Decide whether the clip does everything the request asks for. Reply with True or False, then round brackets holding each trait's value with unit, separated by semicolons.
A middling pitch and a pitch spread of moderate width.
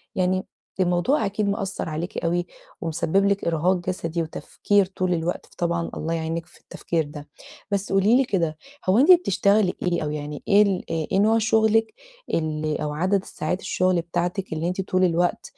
True (180 Hz; 3.3 semitones)